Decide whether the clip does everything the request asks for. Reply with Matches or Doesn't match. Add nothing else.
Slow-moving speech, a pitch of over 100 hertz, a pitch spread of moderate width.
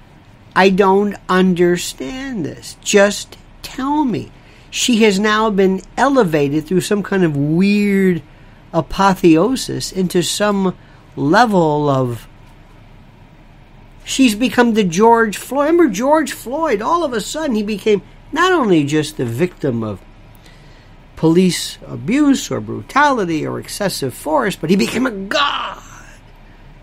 Doesn't match